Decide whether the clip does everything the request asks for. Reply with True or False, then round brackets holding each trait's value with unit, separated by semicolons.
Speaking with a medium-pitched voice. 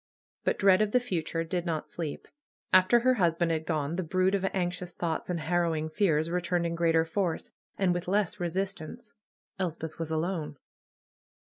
True (175 Hz)